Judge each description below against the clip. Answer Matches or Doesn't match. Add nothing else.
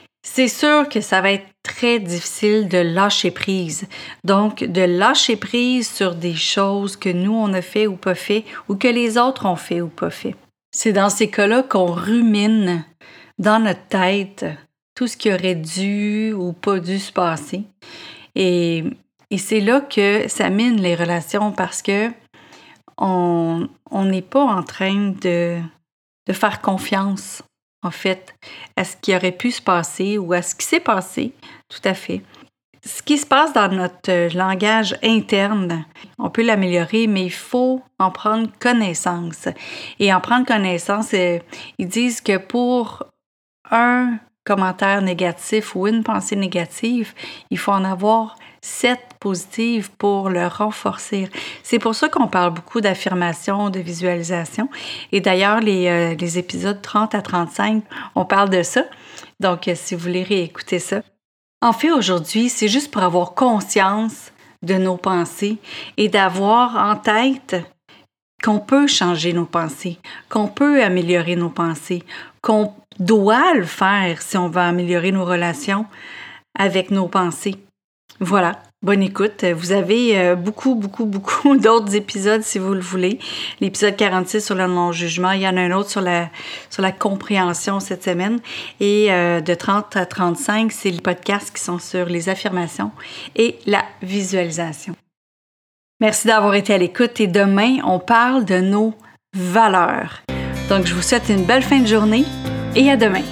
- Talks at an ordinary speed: Matches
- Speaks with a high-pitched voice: Matches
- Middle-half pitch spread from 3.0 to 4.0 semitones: Matches